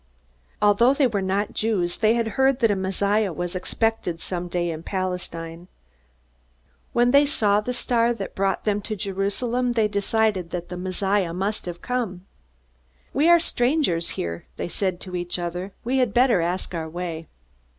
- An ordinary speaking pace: Yes, average, 170 wpm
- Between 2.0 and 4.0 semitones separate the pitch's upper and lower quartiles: No, average, 4.6 semitones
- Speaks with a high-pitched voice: Yes, high, 195 Hz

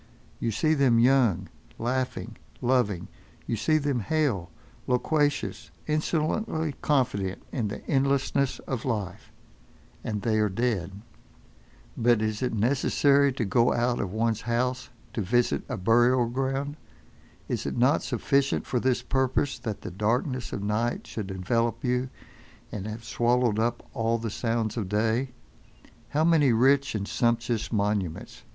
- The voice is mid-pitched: No, low, 120 Hz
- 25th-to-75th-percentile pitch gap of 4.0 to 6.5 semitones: No, average, 3.5 semitones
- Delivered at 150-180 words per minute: No, average, 140 wpm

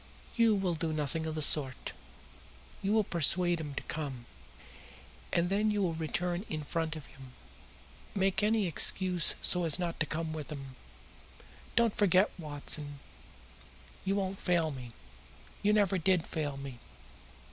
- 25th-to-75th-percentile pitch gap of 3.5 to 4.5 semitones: Yes, average, 4.1 semitones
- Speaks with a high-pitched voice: No, medium, 165 Hz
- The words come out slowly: No, average, 150 wpm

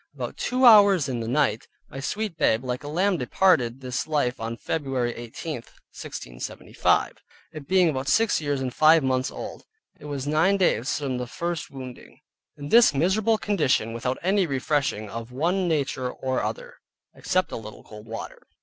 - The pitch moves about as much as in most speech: No, wide, 5.9 semitones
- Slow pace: No, average, 170 wpm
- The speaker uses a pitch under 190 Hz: Yes, medium, 140 Hz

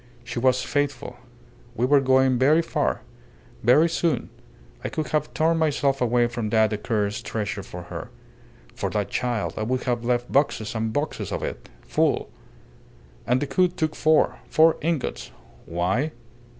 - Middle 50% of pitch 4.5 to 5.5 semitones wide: Yes, average, 5.1 semitones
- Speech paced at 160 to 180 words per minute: No, average, 150 wpm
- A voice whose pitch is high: No, low, 125 Hz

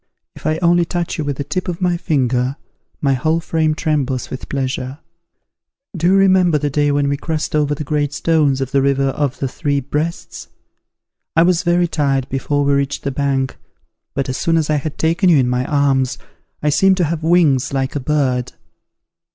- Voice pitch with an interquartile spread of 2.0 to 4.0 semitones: Yes, average, 3.1 semitones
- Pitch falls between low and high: Yes, medium, 145 Hz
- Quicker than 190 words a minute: Yes, average, 200 wpm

